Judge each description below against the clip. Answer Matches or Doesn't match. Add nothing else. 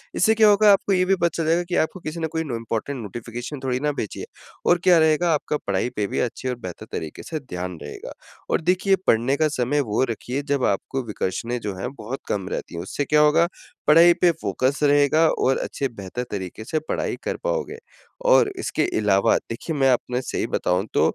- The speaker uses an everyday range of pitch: Doesn't match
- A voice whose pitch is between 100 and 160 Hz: Matches